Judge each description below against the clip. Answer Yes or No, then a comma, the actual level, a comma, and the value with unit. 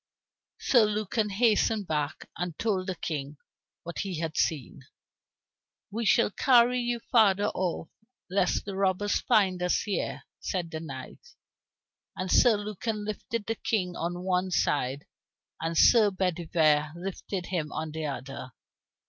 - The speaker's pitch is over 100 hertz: Yes, medium, 185 Hz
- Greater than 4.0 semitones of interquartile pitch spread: Yes, average, 4.6 semitones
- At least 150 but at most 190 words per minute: No, average, 140 wpm